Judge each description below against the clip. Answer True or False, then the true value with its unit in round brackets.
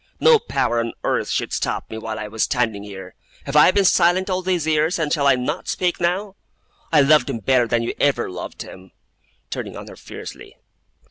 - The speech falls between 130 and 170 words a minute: False (205 wpm)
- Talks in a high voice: False (140 Hz)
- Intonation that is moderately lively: False (7.3 semitones)